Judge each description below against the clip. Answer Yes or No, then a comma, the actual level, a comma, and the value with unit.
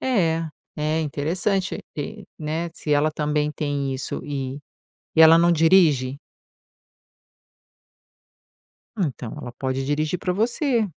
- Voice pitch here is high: No, medium, 155 Hz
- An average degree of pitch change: Yes, average, 3.4 semitones